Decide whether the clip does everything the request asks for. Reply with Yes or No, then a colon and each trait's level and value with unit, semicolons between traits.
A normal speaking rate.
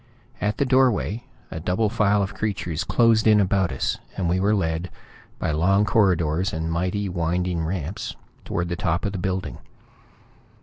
Yes: average, 165 wpm